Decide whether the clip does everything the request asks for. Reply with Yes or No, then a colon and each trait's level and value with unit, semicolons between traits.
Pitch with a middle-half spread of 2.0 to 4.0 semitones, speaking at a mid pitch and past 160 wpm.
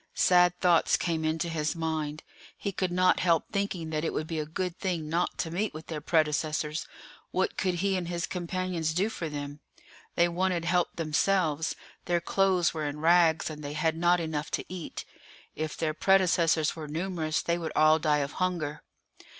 Yes: narrow, 2.4 semitones; medium, 165 Hz; average, 185 wpm